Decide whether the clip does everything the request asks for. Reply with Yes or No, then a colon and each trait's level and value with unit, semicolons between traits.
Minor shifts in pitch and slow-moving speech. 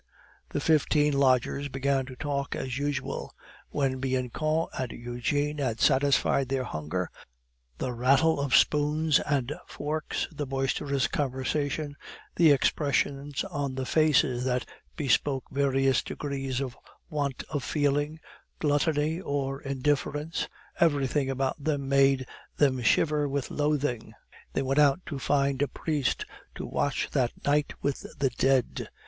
Yes: narrow, 1.8 semitones; slow, 130 wpm